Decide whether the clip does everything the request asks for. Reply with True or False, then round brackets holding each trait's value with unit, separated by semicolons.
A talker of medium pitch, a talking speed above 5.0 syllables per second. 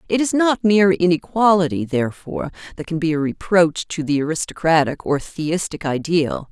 True (170 Hz; 5.3 syllables/s)